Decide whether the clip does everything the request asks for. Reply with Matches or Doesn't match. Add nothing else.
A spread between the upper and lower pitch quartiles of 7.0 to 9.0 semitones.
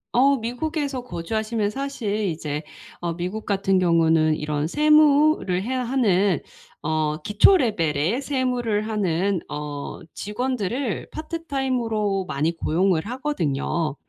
Matches